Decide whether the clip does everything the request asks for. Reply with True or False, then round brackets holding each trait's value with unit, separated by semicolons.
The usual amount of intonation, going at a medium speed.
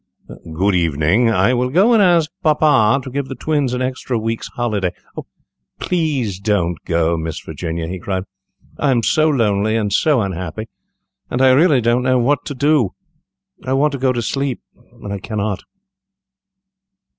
False (5.8 semitones; 165 wpm)